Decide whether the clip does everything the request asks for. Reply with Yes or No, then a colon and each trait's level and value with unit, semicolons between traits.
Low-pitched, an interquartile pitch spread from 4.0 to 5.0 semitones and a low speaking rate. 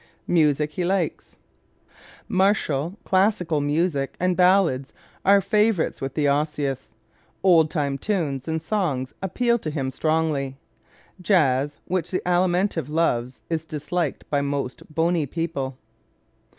No: medium, 160 Hz; average, 4.4 semitones; slow, 125 wpm